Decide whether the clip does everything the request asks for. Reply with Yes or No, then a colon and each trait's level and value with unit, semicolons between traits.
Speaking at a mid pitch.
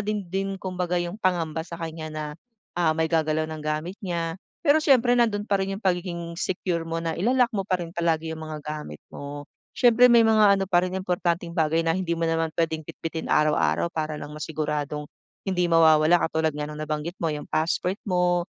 Yes: medium, 170 Hz